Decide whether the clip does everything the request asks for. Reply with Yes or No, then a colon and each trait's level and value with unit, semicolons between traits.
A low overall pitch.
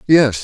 Yes: low, 130 Hz